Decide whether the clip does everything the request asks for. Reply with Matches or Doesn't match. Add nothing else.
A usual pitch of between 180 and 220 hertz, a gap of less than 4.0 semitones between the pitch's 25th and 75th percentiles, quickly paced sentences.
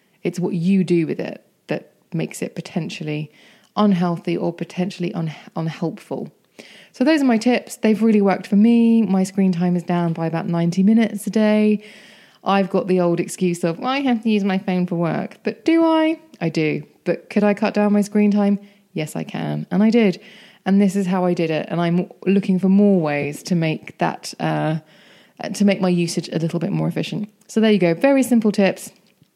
Matches